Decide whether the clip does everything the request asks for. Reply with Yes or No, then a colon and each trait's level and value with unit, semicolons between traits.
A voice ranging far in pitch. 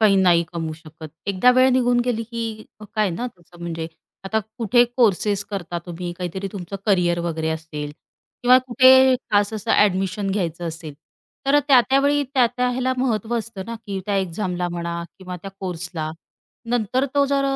Yes: wide, 5.7 semitones